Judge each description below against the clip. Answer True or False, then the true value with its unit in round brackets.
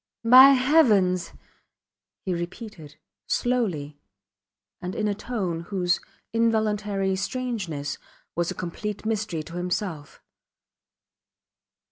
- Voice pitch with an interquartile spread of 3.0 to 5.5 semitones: True (4.5 semitones)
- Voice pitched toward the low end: False (195 Hz)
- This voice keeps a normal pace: False (90 wpm)